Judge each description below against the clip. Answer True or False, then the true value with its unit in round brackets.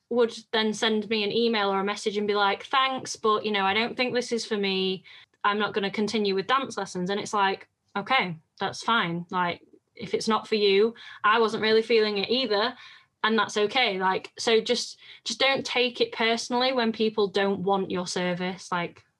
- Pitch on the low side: False (215 Hz)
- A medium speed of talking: False (210 wpm)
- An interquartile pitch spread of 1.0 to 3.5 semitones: True (2.9 semitones)